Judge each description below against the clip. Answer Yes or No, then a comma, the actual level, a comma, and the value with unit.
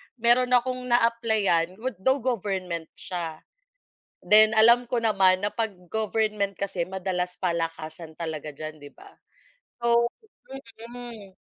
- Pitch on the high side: Yes, high, 200 Hz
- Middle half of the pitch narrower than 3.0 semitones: No, average, 5.1 semitones